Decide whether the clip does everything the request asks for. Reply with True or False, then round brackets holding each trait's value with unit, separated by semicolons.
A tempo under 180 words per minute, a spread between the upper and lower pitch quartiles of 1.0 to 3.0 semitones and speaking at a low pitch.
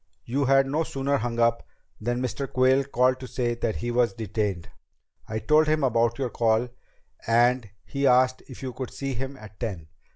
False (190 wpm; 2.6 semitones; 125 Hz)